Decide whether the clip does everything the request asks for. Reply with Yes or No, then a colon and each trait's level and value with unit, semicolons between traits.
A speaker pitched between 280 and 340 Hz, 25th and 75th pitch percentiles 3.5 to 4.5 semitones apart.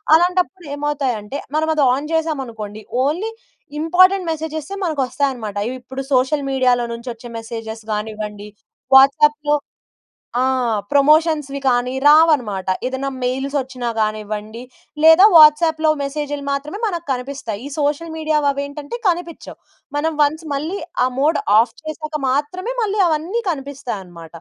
Yes: very high, 285 Hz; average, 4.2 semitones